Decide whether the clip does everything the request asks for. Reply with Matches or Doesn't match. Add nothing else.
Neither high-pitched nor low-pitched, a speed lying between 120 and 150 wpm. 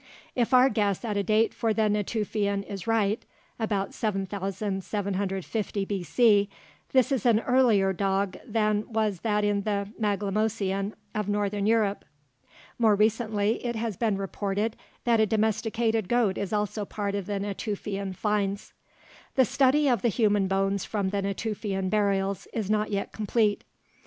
Doesn't match